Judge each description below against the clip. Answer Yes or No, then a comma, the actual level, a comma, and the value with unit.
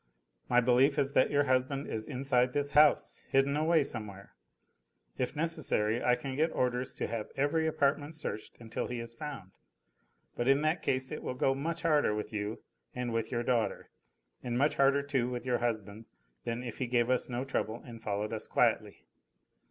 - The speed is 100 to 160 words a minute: No, average, 185 wpm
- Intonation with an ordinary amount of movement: Yes, average, 3.3 semitones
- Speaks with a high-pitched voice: No, low, 125 Hz